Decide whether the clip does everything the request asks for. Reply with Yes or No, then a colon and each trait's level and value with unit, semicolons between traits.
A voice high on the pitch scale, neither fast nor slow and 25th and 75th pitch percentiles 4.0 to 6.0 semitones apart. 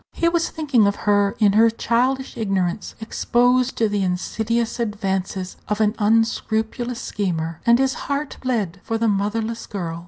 No: high, 220 Hz; average, 155 wpm; average, 3.0 semitones